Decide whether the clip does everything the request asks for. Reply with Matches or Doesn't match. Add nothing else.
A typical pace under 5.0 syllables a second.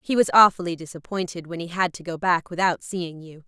Doesn't match